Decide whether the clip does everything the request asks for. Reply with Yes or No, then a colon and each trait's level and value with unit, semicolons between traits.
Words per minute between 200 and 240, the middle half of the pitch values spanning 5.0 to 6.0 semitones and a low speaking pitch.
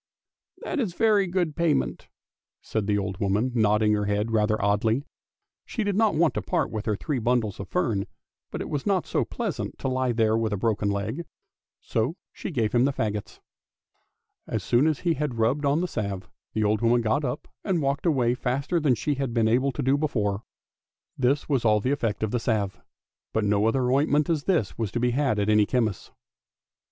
Yes: fast, 205 wpm; wide, 5.4 semitones; low, 120 Hz